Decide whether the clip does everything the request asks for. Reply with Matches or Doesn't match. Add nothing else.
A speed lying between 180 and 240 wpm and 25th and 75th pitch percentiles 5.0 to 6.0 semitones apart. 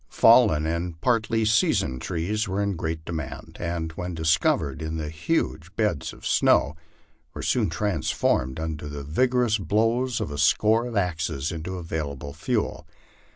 Doesn't match